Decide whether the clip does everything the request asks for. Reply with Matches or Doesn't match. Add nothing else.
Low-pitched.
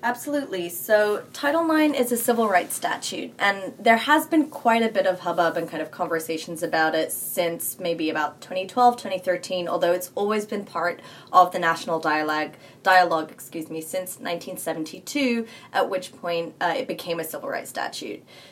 Doesn't match